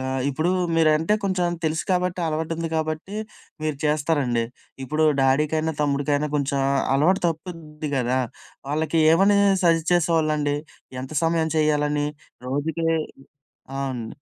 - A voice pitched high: No, medium, 155 Hz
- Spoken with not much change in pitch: Yes, narrow, 2.3 semitones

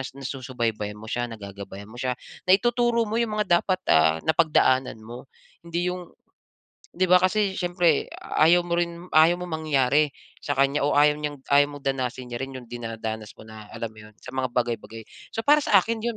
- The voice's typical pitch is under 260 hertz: Yes, medium, 140 Hz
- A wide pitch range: Yes, wide, 6.7 semitones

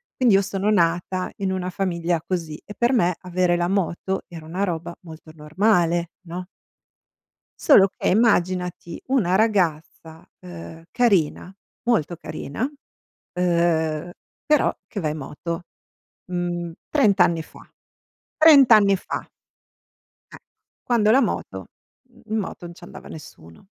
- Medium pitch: Yes, medium, 180 Hz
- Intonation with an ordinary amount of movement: Yes, average, 3.3 semitones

